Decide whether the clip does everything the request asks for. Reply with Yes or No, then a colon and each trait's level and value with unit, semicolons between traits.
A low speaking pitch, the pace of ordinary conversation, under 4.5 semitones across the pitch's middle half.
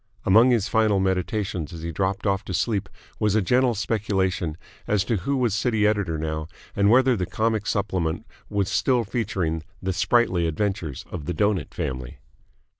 Yes: low, 100 Hz; average, 170 wpm; average, 3.7 semitones